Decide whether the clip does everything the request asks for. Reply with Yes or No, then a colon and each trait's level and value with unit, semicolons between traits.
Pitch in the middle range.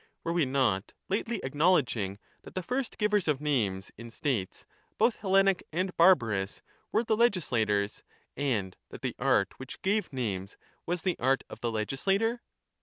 Yes: medium, 145 Hz